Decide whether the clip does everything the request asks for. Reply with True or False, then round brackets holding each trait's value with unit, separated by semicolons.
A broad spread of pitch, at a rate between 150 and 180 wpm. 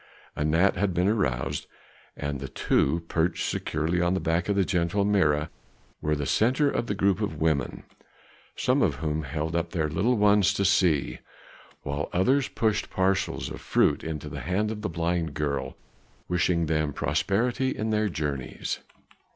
False (4.7 semitones; 165 wpm)